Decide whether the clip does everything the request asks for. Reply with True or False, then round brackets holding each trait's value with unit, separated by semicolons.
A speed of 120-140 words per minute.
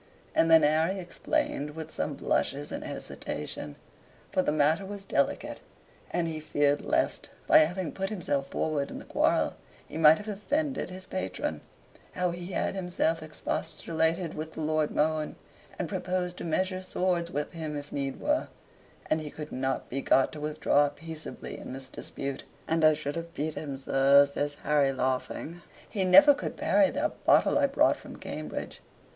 False (170 wpm)